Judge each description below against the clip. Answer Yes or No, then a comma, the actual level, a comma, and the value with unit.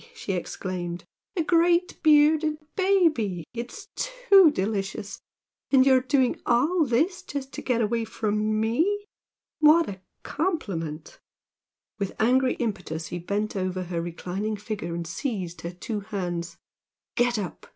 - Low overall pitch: No, high, 225 Hz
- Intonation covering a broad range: Yes, wide, 8.4 semitones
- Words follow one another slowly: Yes, slow, 130 wpm